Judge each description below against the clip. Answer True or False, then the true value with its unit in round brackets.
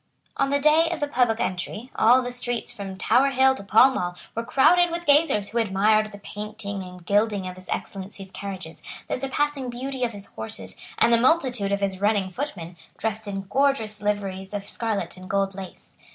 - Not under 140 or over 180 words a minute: False (195 wpm)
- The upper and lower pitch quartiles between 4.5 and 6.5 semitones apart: True (4.9 semitones)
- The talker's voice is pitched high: True (215 Hz)